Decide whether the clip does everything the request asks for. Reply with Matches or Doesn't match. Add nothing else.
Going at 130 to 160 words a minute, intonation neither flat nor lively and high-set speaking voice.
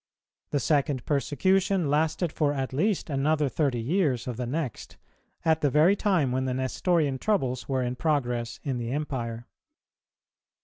Doesn't match